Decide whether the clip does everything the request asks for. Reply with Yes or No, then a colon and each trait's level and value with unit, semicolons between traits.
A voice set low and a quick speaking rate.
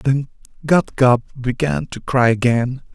No: low, 130 Hz; average, 145 wpm